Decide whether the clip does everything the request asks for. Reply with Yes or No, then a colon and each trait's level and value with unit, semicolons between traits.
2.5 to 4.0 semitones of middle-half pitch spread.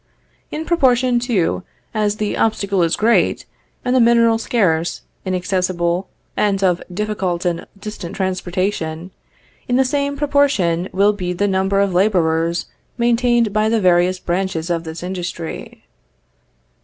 No: average, 4.4 semitones